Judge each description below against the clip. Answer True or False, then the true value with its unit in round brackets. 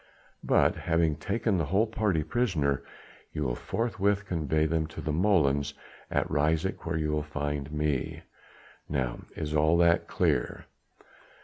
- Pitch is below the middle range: True (80 Hz)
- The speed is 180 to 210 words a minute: False (140 wpm)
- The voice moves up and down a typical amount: True (3.6 semitones)